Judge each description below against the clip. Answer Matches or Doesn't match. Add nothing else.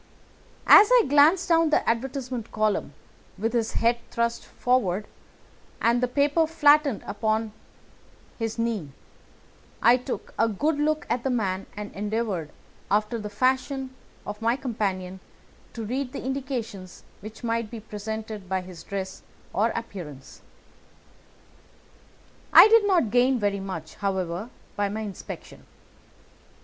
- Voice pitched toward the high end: Matches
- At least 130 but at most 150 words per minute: Matches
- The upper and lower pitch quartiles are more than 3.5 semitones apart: Matches